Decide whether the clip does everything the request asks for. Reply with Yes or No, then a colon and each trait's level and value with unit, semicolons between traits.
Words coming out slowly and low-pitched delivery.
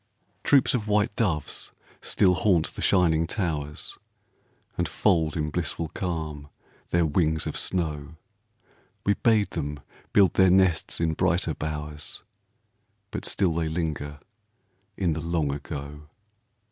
Yes: slow, 125 wpm; very low, 80 Hz